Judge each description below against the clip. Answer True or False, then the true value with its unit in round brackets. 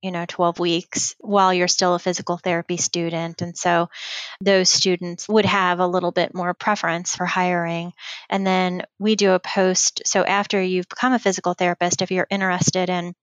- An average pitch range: False (1.4 semitones)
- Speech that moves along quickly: False (185 wpm)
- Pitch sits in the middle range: True (180 Hz)